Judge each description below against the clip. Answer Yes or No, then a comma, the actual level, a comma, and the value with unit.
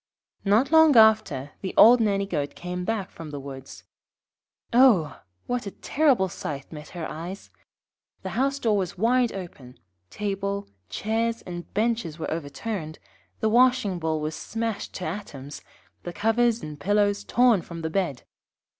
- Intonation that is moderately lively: No, wide, 6.0 semitones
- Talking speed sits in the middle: Yes, average, 150 wpm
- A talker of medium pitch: No, high, 200 Hz